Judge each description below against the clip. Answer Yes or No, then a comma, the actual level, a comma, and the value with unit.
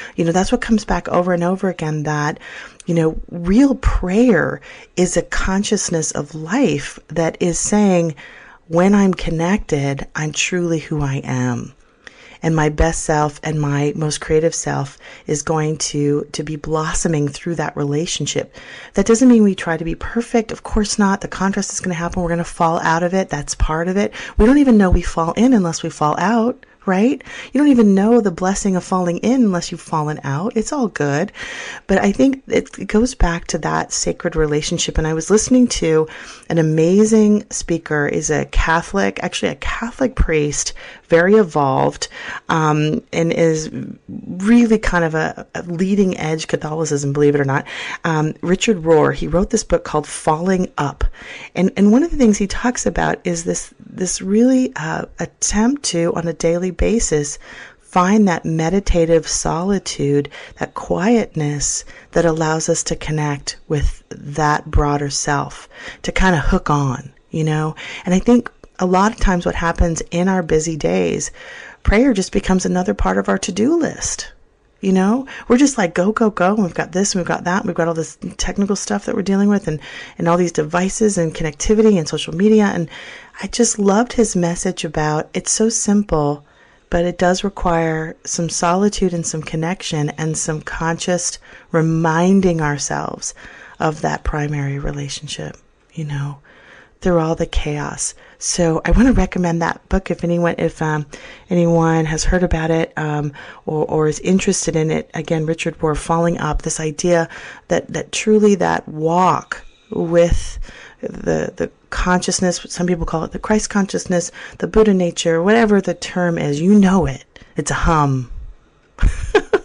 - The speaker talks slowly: No, average, 175 wpm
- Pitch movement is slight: No, average, 4.2 semitones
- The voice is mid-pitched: Yes, medium, 170 Hz